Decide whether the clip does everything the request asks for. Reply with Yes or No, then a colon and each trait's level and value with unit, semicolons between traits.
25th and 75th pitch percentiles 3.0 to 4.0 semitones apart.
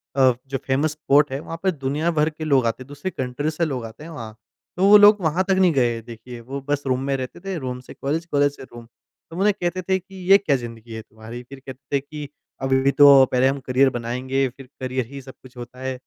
Yes: average, 3.5 semitones